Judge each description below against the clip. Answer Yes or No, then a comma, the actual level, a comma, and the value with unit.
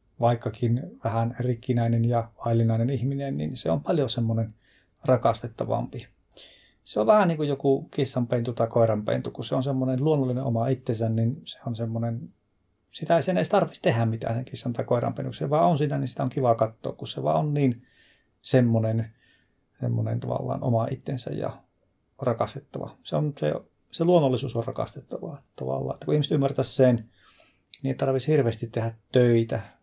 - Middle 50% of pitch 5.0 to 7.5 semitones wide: No, average, 2.9 semitones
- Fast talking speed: Yes, fast, 165 wpm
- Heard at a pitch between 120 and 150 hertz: Yes, low, 125 Hz